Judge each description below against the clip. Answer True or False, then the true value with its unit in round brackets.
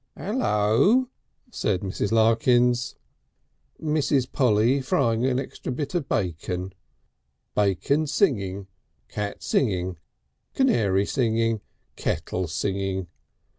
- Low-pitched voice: True (115 Hz)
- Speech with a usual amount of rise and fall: False (5.7 semitones)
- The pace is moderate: False (90 wpm)